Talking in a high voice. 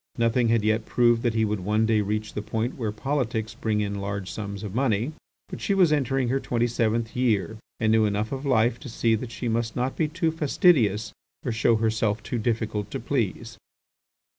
No: low, 115 Hz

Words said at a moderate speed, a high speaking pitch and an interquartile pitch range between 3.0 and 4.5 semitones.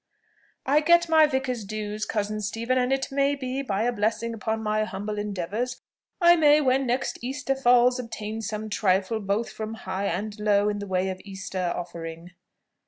Yes: average, 175 wpm; high, 220 Hz; average, 4.0 semitones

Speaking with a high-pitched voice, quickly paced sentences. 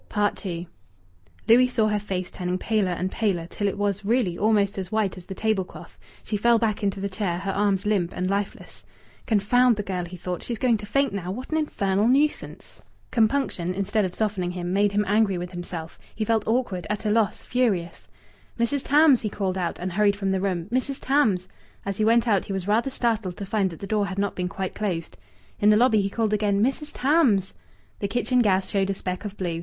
Yes: high, 200 Hz; fast, 220 wpm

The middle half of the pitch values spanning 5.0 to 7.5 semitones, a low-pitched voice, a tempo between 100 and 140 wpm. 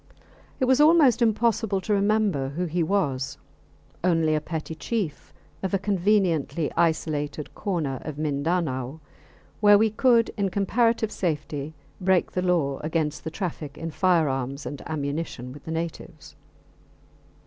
No: average, 5.3 semitones; medium, 165 Hz; slow, 135 wpm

